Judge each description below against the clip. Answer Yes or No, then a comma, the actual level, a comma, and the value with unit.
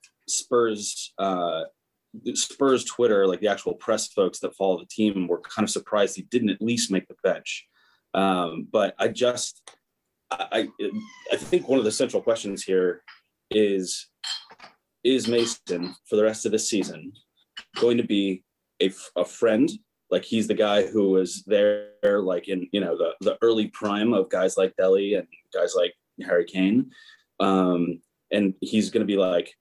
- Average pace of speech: Yes, average, 170 wpm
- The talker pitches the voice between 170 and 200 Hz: No, low, 115 Hz